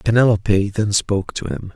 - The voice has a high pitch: No, low, 105 Hz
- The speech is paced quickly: No, average, 170 wpm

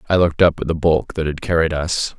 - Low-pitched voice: Yes, very low, 80 Hz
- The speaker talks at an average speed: No, fast, 275 wpm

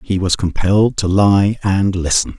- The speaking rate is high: No, average, 175 wpm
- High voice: No, very low, 95 Hz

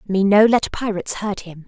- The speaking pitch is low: No, high, 200 Hz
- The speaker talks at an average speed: No, fast, 215 wpm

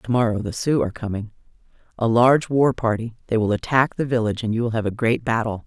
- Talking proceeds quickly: Yes, fast, 210 wpm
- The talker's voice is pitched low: Yes, low, 115 Hz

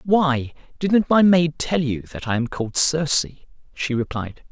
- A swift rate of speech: No, average, 175 wpm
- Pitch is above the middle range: No, medium, 150 Hz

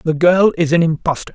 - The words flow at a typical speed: No, fast, 220 wpm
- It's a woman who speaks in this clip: No, male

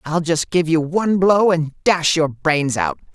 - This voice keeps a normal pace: No, fast, 210 wpm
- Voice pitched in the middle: Yes, medium, 160 Hz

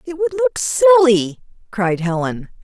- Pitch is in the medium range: No, high, 200 Hz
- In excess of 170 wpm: No, slow, 135 wpm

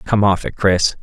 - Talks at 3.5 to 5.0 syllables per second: Yes, 4.5 syllables/s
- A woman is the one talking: No, male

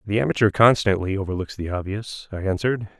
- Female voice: No, male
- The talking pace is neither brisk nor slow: Yes, average, 160 wpm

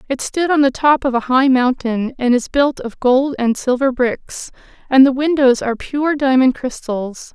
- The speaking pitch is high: Yes, very high, 265 Hz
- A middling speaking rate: Yes, average, 195 wpm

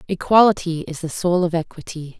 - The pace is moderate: Yes, average, 165 wpm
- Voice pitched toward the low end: No, medium, 170 Hz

